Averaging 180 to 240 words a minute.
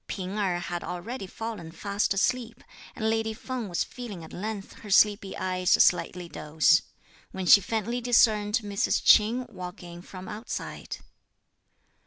No: average, 145 wpm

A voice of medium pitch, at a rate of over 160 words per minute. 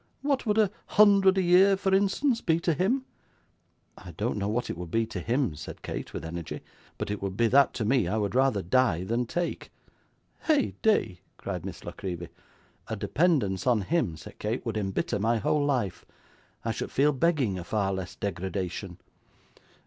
No: low, 120 Hz; average, 185 wpm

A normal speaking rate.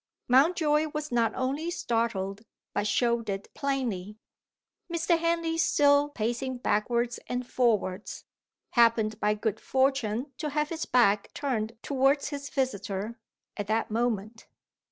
No: slow, 125 wpm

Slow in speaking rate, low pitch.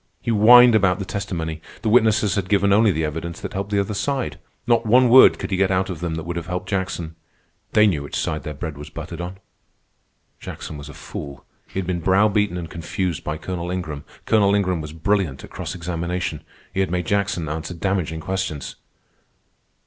No: fast, 205 wpm; very low, 90 Hz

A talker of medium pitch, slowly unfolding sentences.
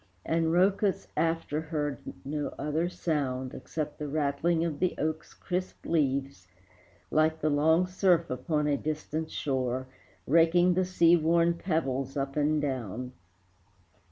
Yes: medium, 155 Hz; slow, 130 wpm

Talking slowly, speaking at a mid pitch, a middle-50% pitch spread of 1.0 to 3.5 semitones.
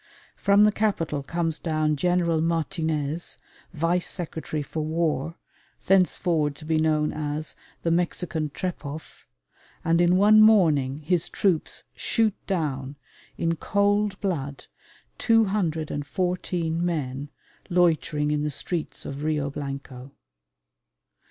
Yes: slow, 110 wpm; medium, 160 Hz; average, 3.2 semitones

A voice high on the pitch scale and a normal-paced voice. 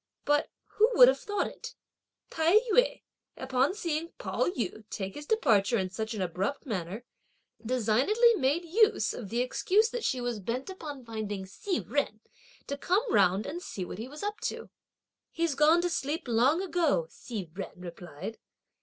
Yes: very high, 260 Hz; average, 170 wpm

